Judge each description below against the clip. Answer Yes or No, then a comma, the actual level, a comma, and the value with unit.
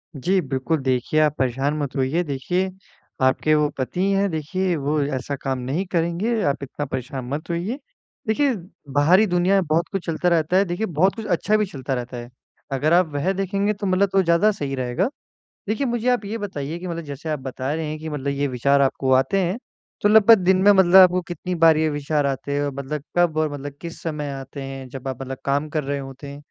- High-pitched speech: No, medium, 155 Hz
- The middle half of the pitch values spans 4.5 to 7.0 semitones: Yes, average, 5.1 semitones